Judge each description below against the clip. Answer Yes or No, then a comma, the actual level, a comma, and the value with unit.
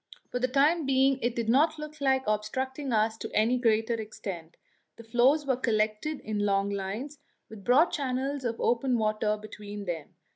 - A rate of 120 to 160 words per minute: No, average, 175 wpm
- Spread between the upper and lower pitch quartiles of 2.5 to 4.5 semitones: Yes, average, 4.0 semitones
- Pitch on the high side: Yes, high, 235 Hz